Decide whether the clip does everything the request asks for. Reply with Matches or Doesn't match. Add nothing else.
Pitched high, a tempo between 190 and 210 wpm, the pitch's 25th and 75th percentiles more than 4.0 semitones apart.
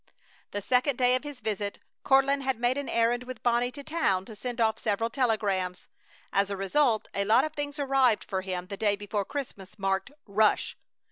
Matches